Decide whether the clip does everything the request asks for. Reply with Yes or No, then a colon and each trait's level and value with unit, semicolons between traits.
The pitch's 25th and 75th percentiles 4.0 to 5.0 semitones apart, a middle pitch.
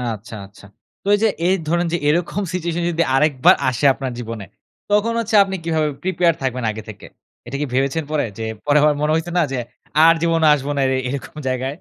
Yes: average, 4.7 semitones; medium, 150 Hz